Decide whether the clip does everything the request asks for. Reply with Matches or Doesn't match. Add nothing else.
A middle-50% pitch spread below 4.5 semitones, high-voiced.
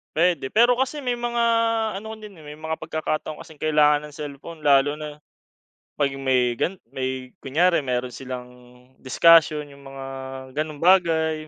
Doesn't match